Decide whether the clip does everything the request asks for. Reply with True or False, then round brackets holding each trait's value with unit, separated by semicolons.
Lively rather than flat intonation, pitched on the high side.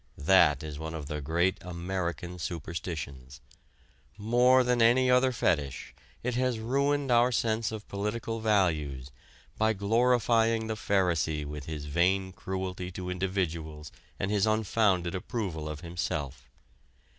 False (5.9 semitones; 95 Hz)